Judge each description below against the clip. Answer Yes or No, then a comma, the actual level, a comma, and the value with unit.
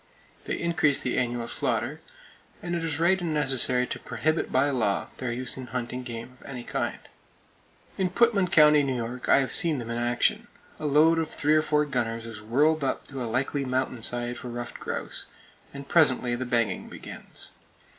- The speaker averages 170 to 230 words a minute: Yes, average, 190 wpm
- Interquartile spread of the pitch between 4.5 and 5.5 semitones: No, average, 4.1 semitones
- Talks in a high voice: No, low, 130 Hz